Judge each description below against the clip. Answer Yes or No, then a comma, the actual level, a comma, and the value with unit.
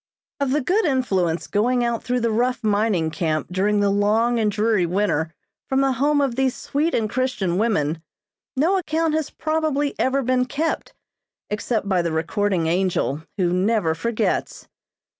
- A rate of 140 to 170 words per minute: Yes, average, 160 wpm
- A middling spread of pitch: No, wide, 6.0 semitones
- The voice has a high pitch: Yes, high, 225 Hz